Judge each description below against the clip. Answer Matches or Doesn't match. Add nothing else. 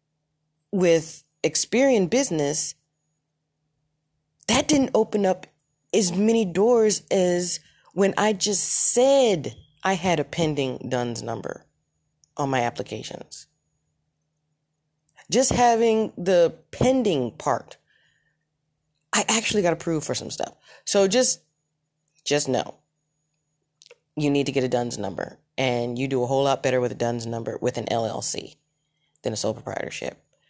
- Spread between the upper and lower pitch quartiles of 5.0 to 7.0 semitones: Matches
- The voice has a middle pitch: Matches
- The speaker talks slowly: Matches